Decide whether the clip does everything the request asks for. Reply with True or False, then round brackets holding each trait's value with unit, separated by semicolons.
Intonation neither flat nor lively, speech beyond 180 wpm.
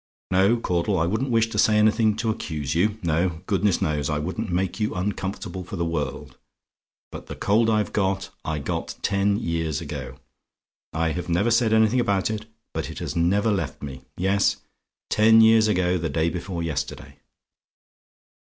False (4.4 semitones; 170 wpm)